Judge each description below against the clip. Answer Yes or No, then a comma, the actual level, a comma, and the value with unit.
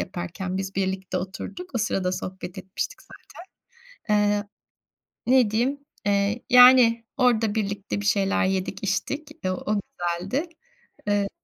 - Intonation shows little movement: No, average, 3.8 semitones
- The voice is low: No, high, 200 Hz